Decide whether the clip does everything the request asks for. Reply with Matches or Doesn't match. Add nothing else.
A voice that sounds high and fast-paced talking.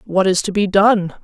Matches